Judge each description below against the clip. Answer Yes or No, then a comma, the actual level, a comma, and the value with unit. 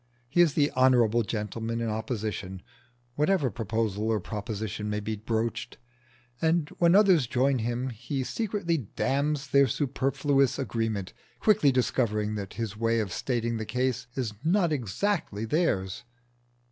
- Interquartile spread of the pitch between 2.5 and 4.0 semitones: No, average, 4.4 semitones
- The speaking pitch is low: Yes, low, 120 Hz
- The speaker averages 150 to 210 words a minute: No, slow, 135 wpm